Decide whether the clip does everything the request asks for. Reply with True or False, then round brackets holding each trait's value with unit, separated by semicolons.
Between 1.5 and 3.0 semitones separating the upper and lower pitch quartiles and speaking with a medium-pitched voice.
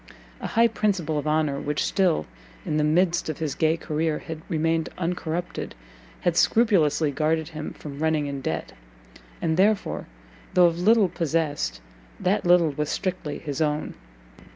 True (2.7 semitones; 160 Hz)